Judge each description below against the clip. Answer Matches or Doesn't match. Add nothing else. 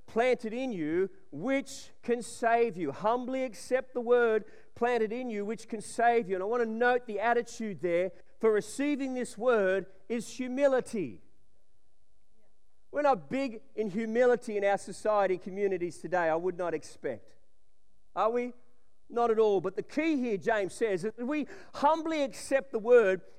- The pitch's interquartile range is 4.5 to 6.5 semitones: Doesn't match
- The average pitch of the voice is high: Matches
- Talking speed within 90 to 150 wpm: Doesn't match